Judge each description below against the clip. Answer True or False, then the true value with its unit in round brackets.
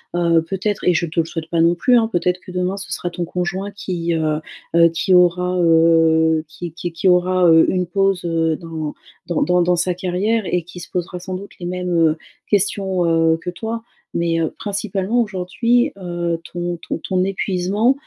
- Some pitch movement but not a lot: False (2.2 semitones)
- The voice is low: False (180 Hz)